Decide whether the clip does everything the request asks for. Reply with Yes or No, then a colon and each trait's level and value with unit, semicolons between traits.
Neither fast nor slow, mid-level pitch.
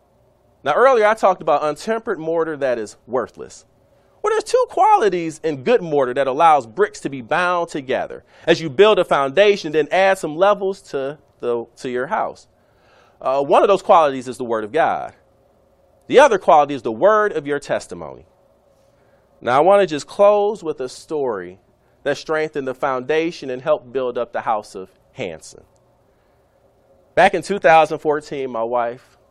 Yes: average, 170 wpm; medium, 155 Hz